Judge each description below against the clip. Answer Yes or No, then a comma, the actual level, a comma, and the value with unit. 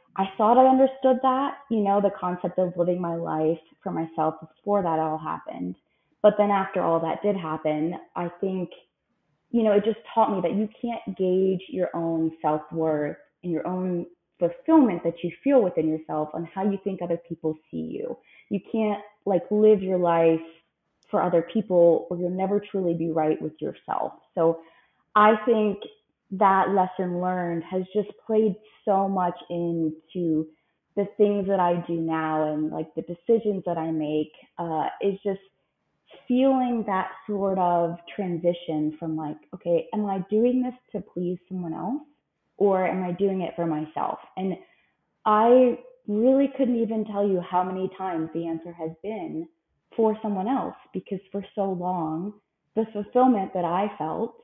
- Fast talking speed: No, average, 170 wpm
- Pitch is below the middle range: No, medium, 185 Hz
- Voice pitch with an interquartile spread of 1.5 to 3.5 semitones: No, average, 4.0 semitones